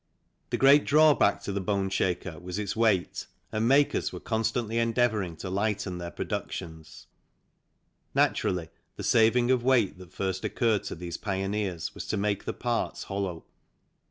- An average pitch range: Yes, average, 4.0 semitones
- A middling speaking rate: Yes, average, 150 wpm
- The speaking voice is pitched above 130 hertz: No, low, 100 Hz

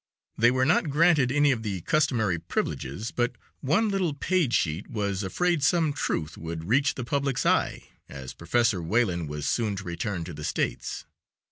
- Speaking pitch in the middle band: No, low, 115 Hz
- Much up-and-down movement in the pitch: Yes, wide, 8.7 semitones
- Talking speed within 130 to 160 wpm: No, average, 170 wpm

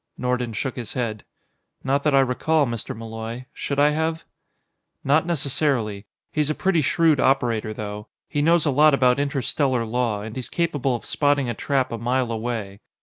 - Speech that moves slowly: No, average, 175 wpm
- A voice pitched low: Yes, low, 130 Hz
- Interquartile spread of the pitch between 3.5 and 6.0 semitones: Yes, average, 4.0 semitones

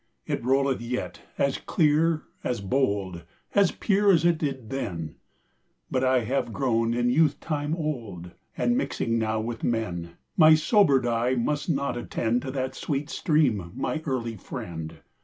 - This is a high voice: No, low, 130 Hz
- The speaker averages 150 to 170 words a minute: No, average, 140 wpm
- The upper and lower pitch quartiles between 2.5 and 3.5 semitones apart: No, average, 4.8 semitones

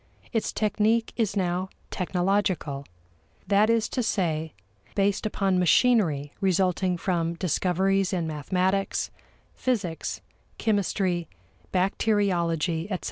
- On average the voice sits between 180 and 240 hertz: Yes, medium, 185 Hz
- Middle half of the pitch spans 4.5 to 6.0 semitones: No, average, 3.0 semitones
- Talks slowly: Yes, slow, 95 wpm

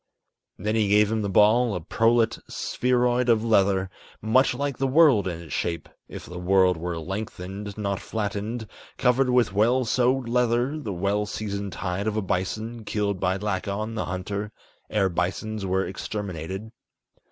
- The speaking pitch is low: Yes, low, 105 Hz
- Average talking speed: Yes, average, 160 wpm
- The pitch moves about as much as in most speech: Yes, average, 3.4 semitones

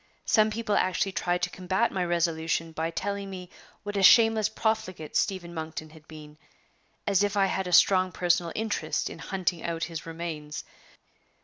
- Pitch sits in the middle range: Yes, medium, 180 Hz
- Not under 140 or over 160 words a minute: No, average, 170 wpm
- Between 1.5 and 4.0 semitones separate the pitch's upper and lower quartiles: Yes, average, 3.5 semitones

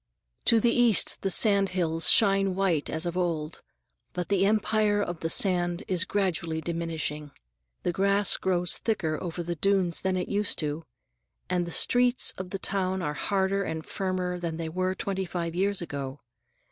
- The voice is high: No, medium, 180 Hz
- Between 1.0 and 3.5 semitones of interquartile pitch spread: Yes, average, 2.9 semitones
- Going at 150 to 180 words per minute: Yes, average, 170 wpm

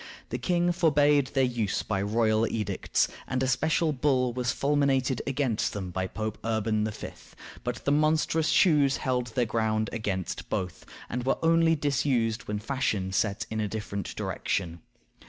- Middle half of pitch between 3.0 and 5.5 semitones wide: Yes, average, 4.8 semitones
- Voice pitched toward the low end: Yes, low, 125 Hz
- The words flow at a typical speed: Yes, average, 155 wpm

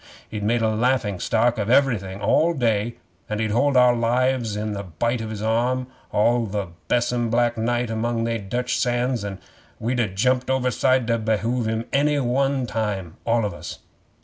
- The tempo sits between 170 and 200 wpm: Yes, average, 180 wpm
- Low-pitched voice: Yes, low, 115 Hz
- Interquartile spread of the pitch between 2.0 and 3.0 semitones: Yes, narrow, 2.5 semitones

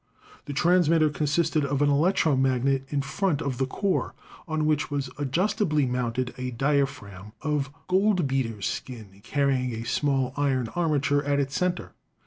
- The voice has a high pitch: No, medium, 140 Hz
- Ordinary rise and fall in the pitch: Yes, average, 3.1 semitones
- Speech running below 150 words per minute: Yes, average, 140 wpm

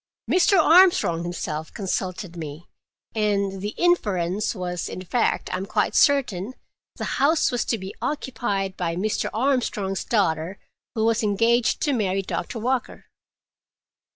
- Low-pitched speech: No, high, 205 Hz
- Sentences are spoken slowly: Yes, slow, 125 wpm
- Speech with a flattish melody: No, average, 4.9 semitones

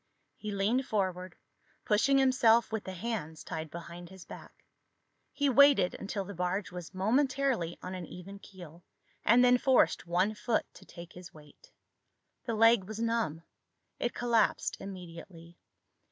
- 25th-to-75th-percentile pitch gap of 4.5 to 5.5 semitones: Yes, average, 4.9 semitones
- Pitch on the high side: Yes, high, 195 Hz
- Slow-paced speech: No, average, 145 wpm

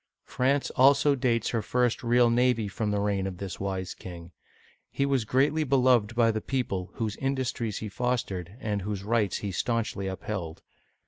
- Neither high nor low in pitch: No, low, 115 Hz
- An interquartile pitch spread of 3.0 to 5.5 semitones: Yes, average, 4.2 semitones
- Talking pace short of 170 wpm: No, average, 175 wpm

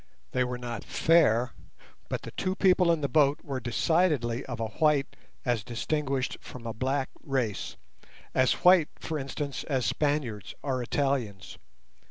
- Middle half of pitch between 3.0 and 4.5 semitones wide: Yes, average, 3.9 semitones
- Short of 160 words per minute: Yes, average, 150 wpm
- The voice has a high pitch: No, low, 135 Hz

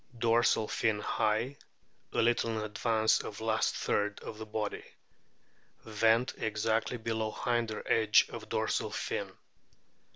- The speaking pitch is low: Yes, low, 110 Hz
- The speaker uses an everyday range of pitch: No, narrow, 1.1 semitones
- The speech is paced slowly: Yes, slow, 120 wpm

